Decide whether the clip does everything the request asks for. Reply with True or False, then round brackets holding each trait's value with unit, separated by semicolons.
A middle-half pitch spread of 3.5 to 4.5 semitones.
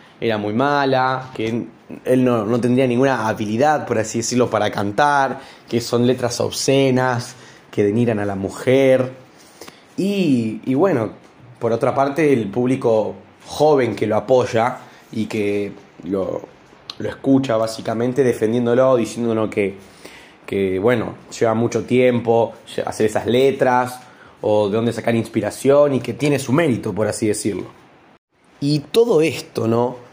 False (2.9 semitones)